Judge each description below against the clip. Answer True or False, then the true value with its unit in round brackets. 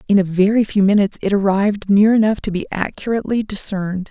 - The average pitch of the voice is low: False (205 Hz)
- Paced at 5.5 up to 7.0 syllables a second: True (6.5 syllables/s)